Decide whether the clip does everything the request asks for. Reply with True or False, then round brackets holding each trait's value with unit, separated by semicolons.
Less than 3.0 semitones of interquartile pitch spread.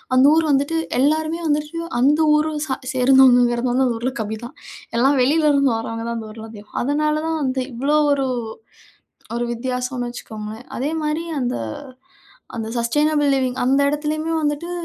False (3.8 semitones)